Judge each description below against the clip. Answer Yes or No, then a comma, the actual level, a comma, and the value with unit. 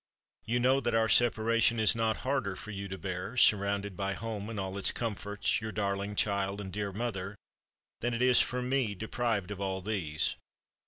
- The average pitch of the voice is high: No, low, 105 Hz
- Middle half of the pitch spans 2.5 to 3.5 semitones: Yes, average, 2.8 semitones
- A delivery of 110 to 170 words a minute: No, average, 190 wpm